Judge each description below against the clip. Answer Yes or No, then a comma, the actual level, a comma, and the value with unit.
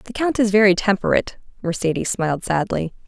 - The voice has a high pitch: Yes, high, 200 Hz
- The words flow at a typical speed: Yes, average, 155 wpm